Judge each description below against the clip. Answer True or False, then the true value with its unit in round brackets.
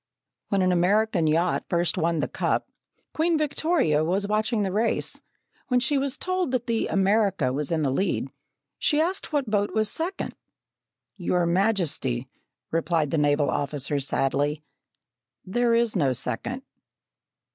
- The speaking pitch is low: False (195 Hz)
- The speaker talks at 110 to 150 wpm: True (145 wpm)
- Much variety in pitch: True (7.3 semitones)